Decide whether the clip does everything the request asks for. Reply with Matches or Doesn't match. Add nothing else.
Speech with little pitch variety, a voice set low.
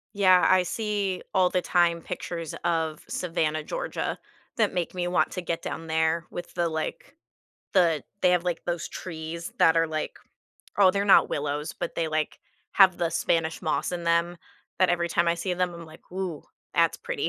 Doesn't match